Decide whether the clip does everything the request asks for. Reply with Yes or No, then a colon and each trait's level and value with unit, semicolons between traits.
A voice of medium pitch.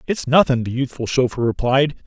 No: low, 130 Hz